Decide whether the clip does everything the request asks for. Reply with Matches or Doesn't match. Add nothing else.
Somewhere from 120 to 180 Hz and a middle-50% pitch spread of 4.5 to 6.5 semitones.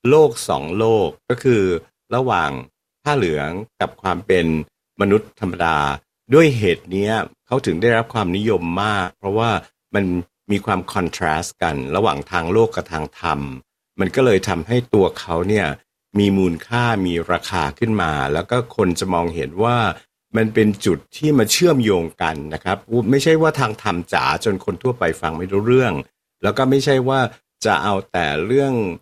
Doesn't match